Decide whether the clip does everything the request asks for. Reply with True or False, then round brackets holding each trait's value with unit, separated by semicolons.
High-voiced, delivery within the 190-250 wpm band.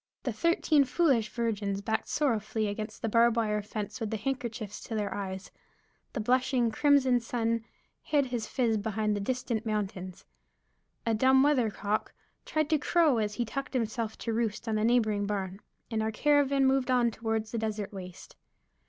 False (225 Hz; 165 wpm)